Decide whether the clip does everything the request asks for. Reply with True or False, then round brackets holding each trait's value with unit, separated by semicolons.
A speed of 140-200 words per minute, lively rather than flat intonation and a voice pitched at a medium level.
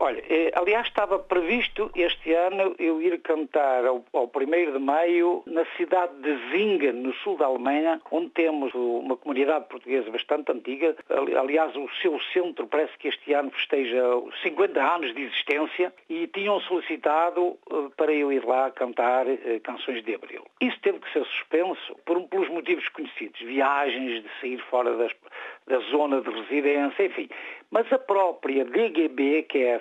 True (160 wpm; 6.4 semitones; 160 Hz)